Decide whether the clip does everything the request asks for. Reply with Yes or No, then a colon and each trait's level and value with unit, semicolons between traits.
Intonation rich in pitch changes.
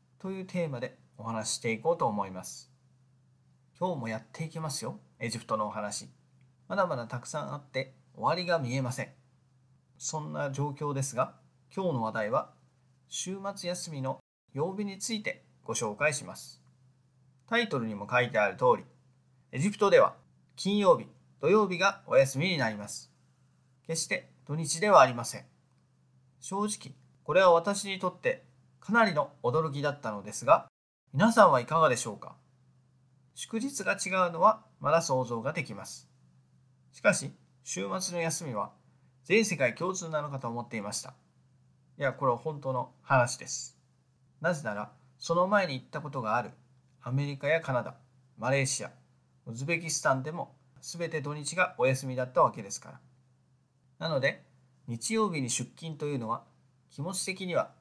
No: average, 5.0 semitones